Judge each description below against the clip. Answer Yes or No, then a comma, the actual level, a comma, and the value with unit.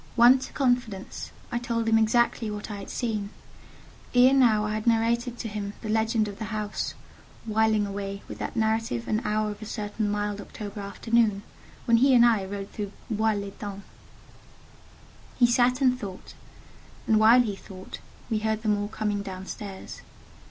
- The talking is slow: No, average, 170 wpm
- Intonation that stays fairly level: Yes, narrow, 2.2 semitones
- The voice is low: No, high, 215 Hz